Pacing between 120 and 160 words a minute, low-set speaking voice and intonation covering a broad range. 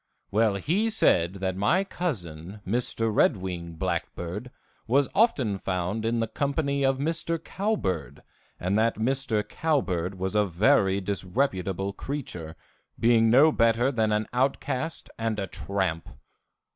Yes: slow, 135 wpm; low, 110 Hz; wide, 6.4 semitones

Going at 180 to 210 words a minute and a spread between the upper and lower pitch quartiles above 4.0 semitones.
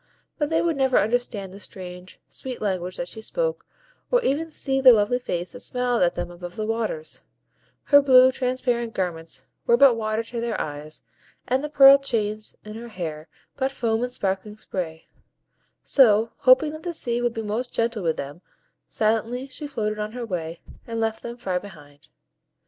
Yes: average, 185 wpm; wide, 5.5 semitones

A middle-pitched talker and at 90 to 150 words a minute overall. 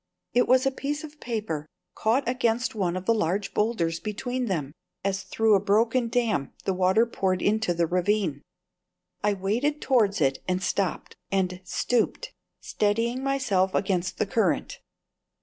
No: high, 210 Hz; average, 145 wpm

